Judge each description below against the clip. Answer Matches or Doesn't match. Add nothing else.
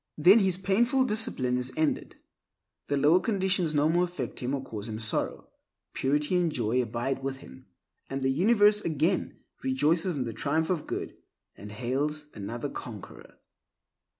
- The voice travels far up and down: Matches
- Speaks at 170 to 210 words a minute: Doesn't match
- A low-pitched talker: Doesn't match